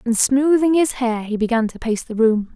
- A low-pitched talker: No, high, 245 Hz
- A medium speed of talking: No, fast, 235 wpm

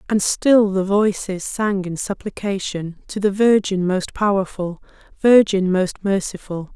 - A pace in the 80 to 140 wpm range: Yes, slow, 135 wpm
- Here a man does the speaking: No, female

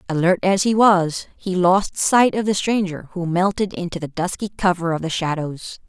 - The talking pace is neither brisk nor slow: Yes, average, 195 wpm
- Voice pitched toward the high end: No, medium, 180 Hz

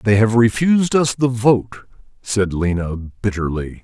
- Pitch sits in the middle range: No, low, 110 Hz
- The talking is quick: No, average, 140 wpm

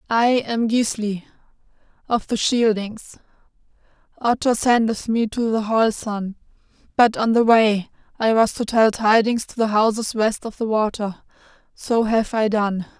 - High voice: Yes, high, 220 Hz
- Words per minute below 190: Yes, average, 150 wpm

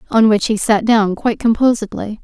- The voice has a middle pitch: No, high, 220 Hz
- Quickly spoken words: No, average, 190 wpm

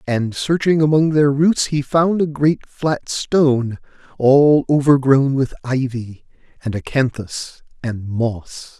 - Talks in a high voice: No, low, 135 Hz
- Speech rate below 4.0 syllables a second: Yes, 3.6 syllables/s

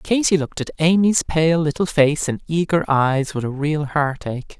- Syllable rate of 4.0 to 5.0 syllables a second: Yes, 4.8 syllables/s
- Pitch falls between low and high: Yes, medium, 155 Hz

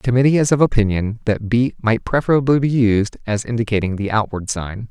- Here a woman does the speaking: No, male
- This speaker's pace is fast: No, average, 195 wpm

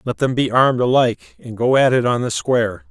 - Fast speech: Yes, fast, 250 wpm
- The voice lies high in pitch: No, low, 125 Hz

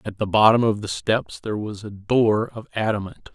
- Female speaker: No, male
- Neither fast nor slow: No, fast, 215 wpm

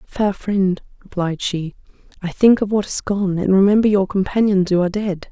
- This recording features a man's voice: No, female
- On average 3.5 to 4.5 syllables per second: No, 5.1 syllables/s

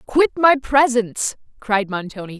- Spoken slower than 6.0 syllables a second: Yes, 4.5 syllables/s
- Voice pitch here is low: No, high, 235 Hz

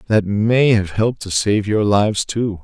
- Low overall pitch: Yes, low, 105 Hz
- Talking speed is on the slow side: No, fast, 205 wpm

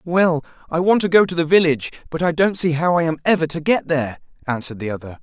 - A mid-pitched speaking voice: Yes, medium, 160 Hz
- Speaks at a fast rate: Yes, fast, 255 wpm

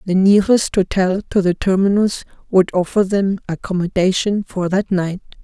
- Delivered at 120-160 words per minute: Yes, average, 145 wpm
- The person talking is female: Yes, female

